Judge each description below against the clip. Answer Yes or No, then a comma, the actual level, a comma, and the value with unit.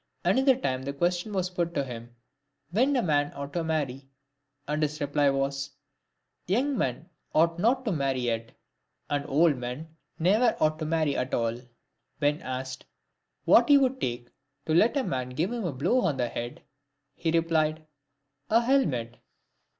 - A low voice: No, medium, 155 Hz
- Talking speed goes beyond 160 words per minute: Yes, average, 170 wpm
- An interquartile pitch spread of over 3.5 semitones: Yes, average, 5.3 semitones